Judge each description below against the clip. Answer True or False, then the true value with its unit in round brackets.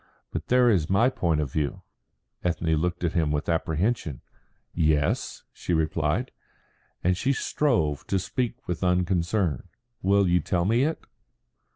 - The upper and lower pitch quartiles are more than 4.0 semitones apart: True (4.8 semitones)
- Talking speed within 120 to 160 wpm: True (145 wpm)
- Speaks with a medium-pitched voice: False (90 Hz)